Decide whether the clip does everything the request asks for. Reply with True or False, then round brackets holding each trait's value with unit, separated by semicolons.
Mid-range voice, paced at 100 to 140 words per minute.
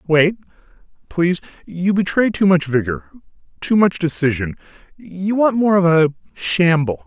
True (170 Hz; 135 wpm)